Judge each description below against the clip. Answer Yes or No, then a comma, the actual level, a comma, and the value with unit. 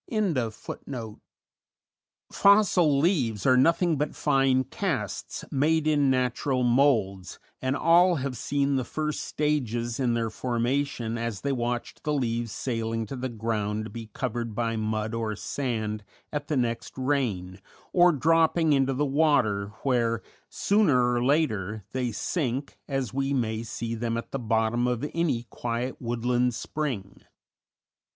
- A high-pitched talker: No, low, 125 Hz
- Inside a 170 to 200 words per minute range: No, average, 140 wpm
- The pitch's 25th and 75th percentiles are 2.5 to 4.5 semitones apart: Yes, average, 3.8 semitones